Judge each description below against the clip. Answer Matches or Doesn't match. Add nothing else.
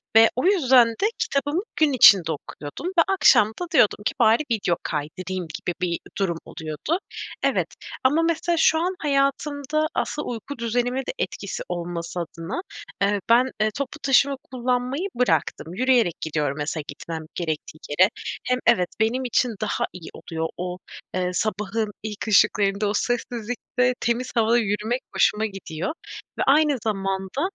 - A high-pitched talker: Matches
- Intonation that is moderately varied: Doesn't match